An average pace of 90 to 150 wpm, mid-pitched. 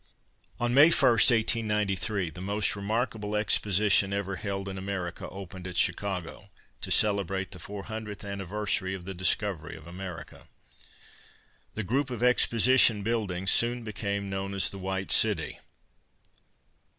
No: slow, 135 wpm; low, 100 Hz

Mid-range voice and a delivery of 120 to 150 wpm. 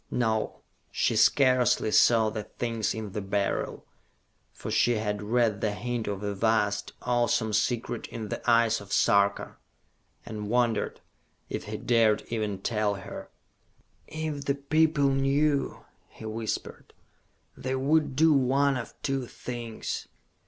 No: low, 115 Hz; slow, 135 wpm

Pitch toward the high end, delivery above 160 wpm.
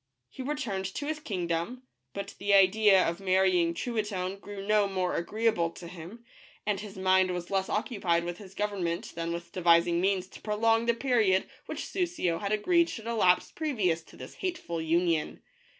Yes: high, 195 Hz; average, 180 wpm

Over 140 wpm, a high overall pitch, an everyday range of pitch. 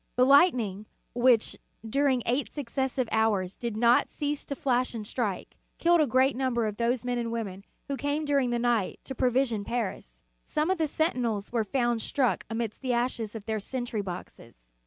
Yes: average, 180 wpm; high, 240 Hz; average, 3.3 semitones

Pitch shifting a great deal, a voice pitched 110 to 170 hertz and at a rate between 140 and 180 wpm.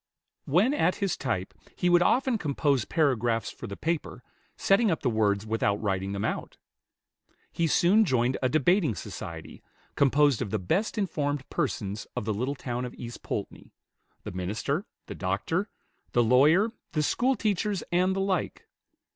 Yes: wide, 8.5 semitones; medium, 140 Hz; average, 155 wpm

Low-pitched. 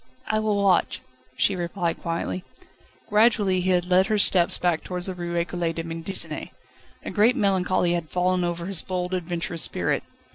No: medium, 180 Hz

